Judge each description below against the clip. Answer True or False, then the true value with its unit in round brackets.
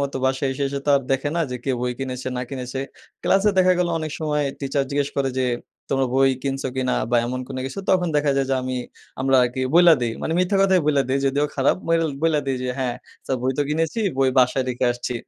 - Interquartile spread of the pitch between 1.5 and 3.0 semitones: True (2.6 semitones)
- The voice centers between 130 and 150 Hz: True (135 Hz)